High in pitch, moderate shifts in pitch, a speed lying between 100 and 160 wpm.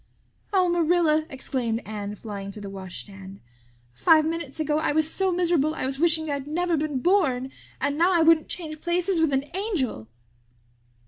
No: very high, 310 Hz; average, 4.9 semitones; average, 170 wpm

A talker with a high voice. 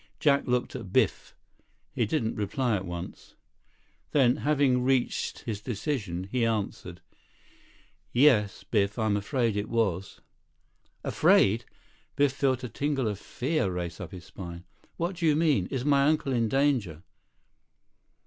No: low, 120 Hz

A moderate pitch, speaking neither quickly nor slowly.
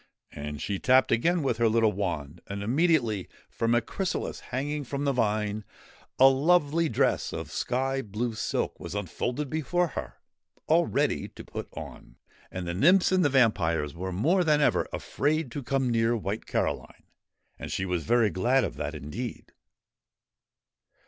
No: low, 120 Hz; average, 160 wpm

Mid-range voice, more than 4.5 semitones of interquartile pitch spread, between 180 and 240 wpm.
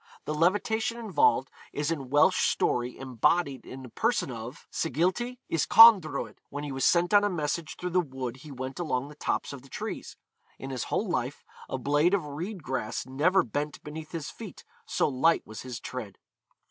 Yes: medium, 145 Hz; average, 5.1 semitones; average, 185 wpm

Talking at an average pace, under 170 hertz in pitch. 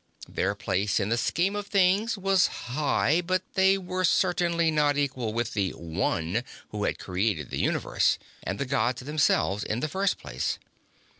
Yes: average, 165 wpm; medium, 140 Hz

